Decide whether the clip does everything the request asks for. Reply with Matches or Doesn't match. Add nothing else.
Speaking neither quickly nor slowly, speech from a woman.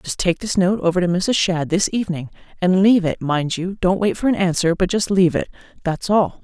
Doesn't match